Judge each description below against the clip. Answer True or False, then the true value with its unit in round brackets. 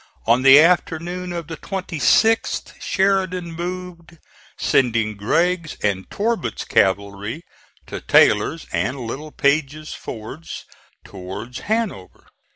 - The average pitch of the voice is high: False (155 Hz)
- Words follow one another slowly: True (95 wpm)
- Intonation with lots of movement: True (7.6 semitones)